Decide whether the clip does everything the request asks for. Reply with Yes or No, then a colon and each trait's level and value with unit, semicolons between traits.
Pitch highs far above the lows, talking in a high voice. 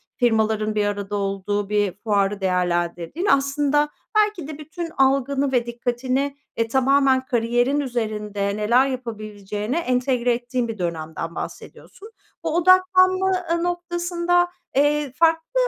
Yes: wide, 6.0 semitones; very high, 250 Hz